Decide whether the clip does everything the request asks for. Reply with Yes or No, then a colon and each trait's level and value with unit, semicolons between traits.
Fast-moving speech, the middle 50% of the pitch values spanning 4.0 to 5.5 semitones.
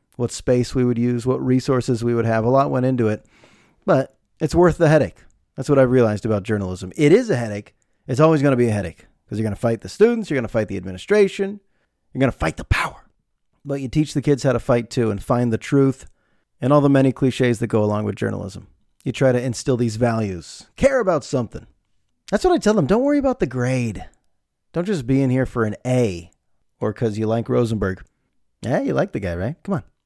Yes: fast, 240 wpm; average, 4.3 semitones